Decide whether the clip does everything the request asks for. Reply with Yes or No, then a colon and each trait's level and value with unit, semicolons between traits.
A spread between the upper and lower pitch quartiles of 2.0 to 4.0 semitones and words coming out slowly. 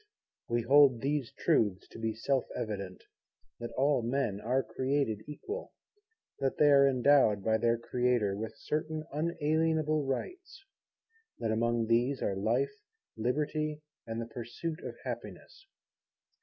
No: average, 4.7 semitones; slow, 130 wpm